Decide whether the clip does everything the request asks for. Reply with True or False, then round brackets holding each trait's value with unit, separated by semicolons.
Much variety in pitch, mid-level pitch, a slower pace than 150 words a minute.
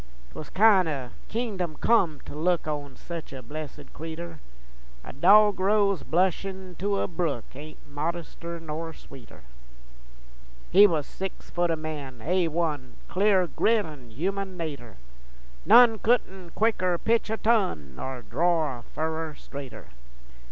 False (4.5 semitones; 170 Hz; 135 wpm)